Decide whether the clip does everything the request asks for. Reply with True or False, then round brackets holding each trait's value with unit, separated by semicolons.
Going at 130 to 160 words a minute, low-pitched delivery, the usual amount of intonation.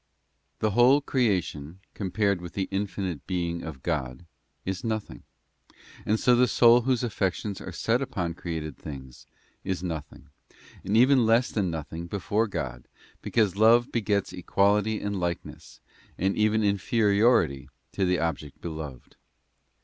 True (155 wpm; 100 Hz; 4.6 semitones)